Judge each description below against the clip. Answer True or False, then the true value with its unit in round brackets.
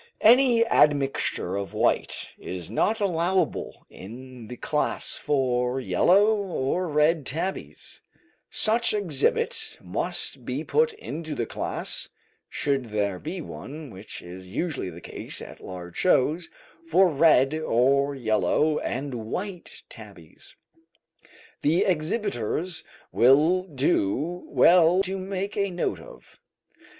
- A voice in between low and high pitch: True (150 Hz)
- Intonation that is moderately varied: False (6.8 semitones)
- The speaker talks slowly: True (115 wpm)